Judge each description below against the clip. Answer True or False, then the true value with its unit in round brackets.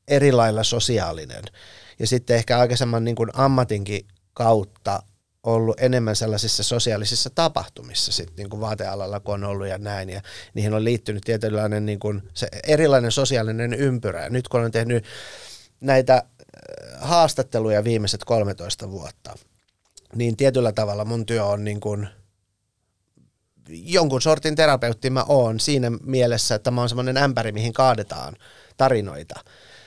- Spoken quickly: False (135 wpm)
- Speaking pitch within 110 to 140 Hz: True (115 Hz)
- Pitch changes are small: False (3.3 semitones)